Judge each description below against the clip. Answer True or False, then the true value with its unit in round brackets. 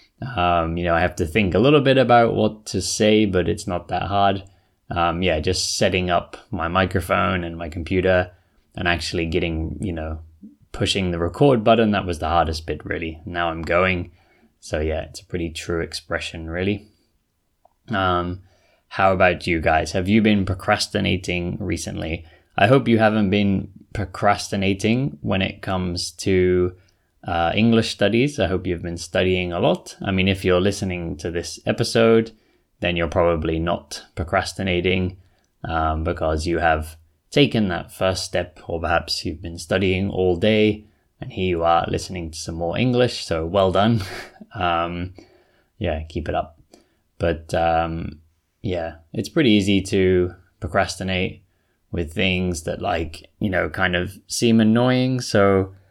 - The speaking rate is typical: True (160 wpm)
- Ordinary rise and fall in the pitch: True (3.2 semitones)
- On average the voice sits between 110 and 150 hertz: False (90 Hz)